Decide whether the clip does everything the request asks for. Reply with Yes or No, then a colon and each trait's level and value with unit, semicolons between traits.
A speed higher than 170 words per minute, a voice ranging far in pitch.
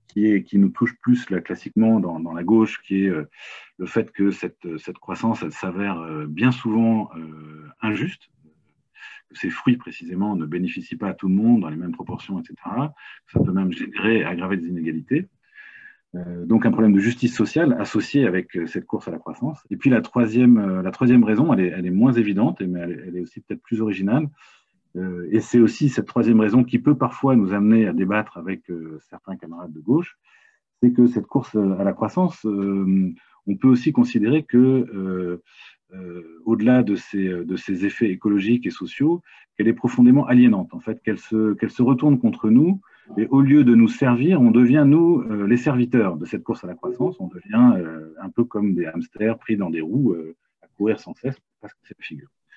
No: average, 200 wpm; average, 4.8 semitones